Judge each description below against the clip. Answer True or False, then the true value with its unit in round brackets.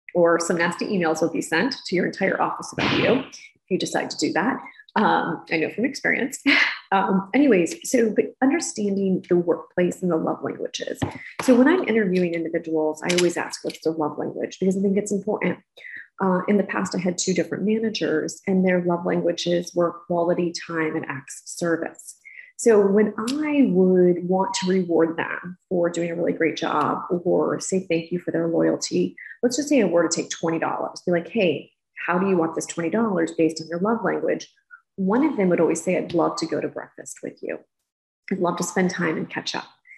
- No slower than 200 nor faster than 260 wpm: True (205 wpm)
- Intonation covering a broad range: False (4.2 semitones)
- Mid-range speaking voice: True (180 Hz)